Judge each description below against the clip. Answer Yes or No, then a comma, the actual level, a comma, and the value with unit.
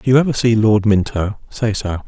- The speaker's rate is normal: No, fast, 230 wpm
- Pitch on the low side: Yes, low, 110 Hz